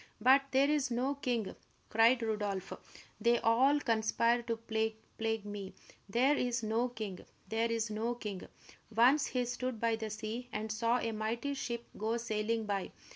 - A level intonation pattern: Yes, narrow, 2.0 semitones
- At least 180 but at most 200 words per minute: No, average, 160 wpm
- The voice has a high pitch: Yes, high, 230 Hz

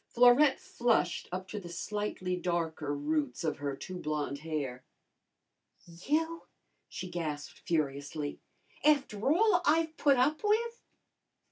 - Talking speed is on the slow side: Yes, slow, 120 wpm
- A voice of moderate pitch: Yes, medium, 180 Hz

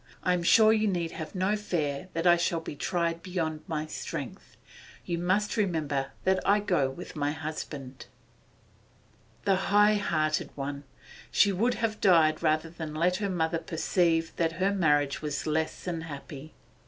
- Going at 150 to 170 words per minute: Yes, average, 165 wpm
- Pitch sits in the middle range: Yes, medium, 165 Hz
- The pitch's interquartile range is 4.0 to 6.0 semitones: No, average, 3.4 semitones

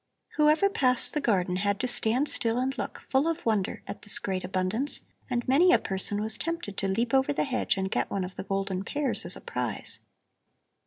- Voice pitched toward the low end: No, high, 230 Hz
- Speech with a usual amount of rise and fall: No, wide, 5.9 semitones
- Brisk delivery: Yes, fast, 210 wpm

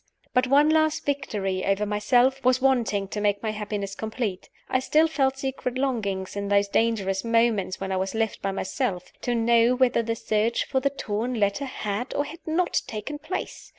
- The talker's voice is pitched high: Yes, high, 230 Hz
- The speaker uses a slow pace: No, average, 185 wpm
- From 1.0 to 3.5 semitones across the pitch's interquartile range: No, average, 4.6 semitones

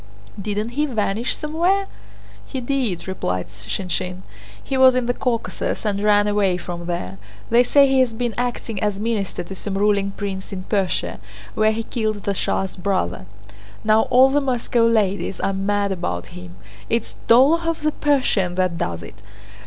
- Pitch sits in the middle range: No, high, 210 Hz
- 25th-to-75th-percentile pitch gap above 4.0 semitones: Yes, average, 4.7 semitones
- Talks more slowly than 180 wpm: Yes, average, 165 wpm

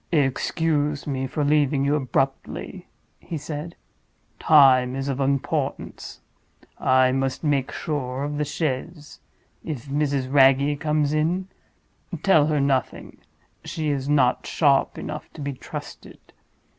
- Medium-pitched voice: Yes, medium, 145 Hz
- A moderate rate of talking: No, slow, 120 wpm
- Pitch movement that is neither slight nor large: No, narrow, 2.1 semitones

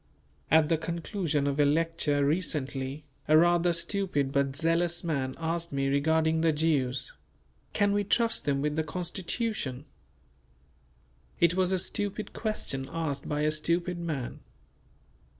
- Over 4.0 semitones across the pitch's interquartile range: No, average, 3.3 semitones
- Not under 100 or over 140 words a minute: Yes, slow, 135 wpm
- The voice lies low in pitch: No, medium, 160 Hz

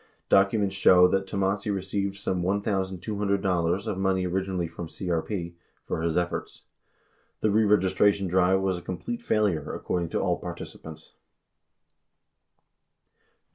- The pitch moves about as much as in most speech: No, narrow, 1.9 semitones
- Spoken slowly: Yes, slow, 115 wpm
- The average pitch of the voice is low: Yes, very low, 95 Hz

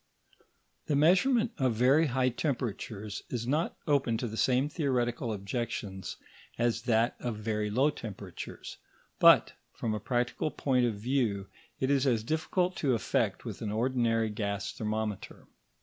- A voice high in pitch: No, low, 120 Hz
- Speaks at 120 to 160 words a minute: Yes, average, 145 wpm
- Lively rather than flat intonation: No, average, 3.7 semitones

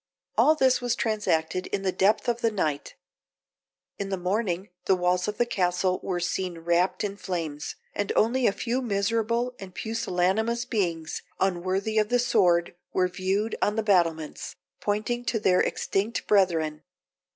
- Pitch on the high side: Yes, high, 195 Hz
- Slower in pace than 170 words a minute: Yes, average, 155 wpm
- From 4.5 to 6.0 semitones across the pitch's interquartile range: No, average, 3.7 semitones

